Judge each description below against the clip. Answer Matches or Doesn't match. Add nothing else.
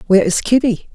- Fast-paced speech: Doesn't match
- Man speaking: Doesn't match